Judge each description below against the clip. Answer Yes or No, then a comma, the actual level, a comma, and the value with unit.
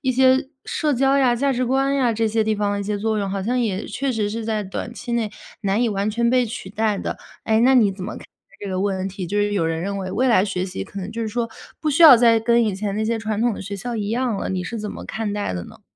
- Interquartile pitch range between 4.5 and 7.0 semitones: No, average, 3.2 semitones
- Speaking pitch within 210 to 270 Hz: Yes, high, 220 Hz